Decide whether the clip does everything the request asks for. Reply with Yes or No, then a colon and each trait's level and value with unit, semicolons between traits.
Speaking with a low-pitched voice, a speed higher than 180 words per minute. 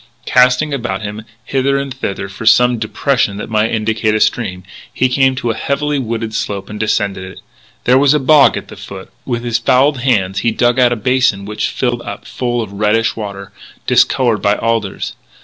Yes: low, 115 Hz; average, 195 wpm